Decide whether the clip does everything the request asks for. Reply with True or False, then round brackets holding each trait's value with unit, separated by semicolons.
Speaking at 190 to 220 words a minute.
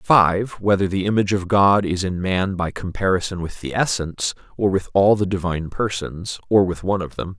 True (205 wpm)